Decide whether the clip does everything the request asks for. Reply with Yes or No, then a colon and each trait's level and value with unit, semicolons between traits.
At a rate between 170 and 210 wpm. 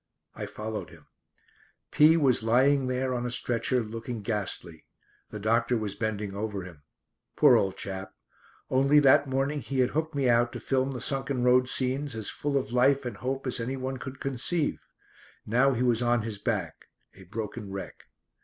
Yes: average, 175 wpm